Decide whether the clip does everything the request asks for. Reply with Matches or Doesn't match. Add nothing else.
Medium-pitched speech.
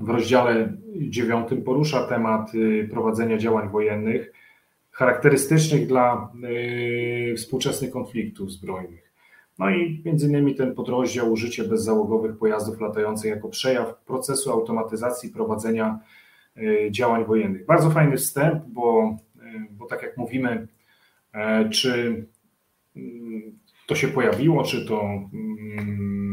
Doesn't match